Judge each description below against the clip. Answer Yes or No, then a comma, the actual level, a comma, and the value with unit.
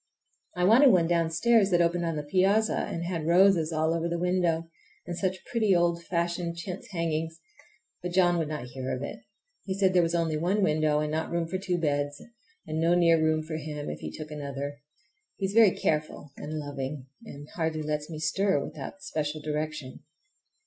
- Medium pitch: Yes, medium, 165 Hz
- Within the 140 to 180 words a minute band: No, average, 195 wpm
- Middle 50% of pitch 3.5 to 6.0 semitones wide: No, average, 2.7 semitones